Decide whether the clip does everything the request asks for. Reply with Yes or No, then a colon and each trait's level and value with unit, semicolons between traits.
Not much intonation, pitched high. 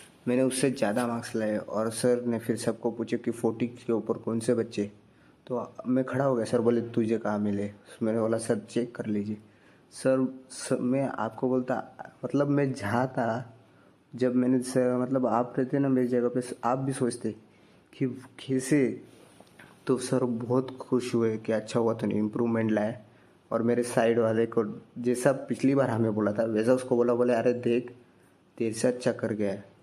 No: narrow, 2.3 semitones; low, 120 Hz